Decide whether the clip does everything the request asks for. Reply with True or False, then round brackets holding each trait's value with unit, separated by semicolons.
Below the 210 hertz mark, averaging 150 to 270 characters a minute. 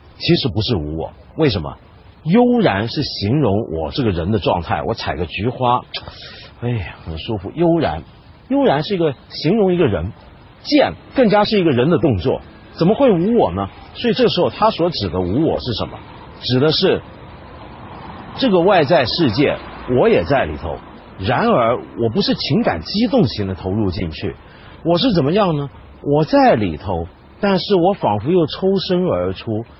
True (135 Hz; 245 characters per minute)